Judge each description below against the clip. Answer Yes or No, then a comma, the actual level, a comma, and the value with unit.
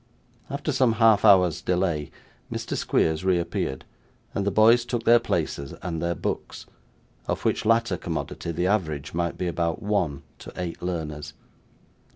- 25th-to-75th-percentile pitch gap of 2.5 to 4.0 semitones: No, average, 5.0 semitones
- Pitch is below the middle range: Yes, very low, 90 Hz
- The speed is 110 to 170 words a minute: Yes, average, 150 wpm